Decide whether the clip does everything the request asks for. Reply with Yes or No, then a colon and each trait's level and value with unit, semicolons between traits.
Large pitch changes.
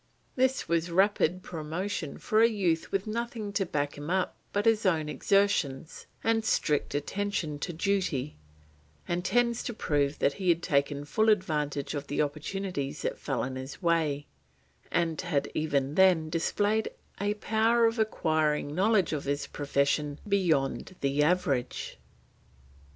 Yes: wide, 5.7 semitones